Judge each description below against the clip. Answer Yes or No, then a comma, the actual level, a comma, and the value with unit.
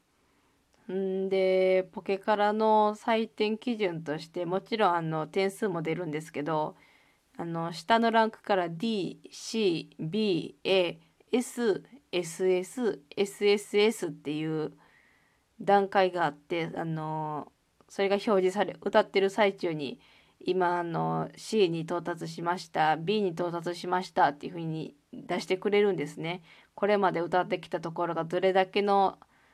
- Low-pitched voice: No, medium, 185 Hz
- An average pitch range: Yes, average, 3.4 semitones